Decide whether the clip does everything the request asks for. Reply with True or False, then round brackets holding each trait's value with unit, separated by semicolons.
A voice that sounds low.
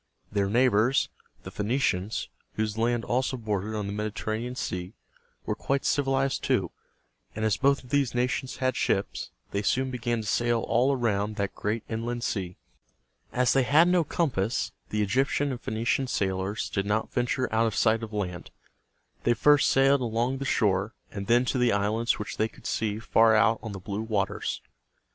True (115 Hz)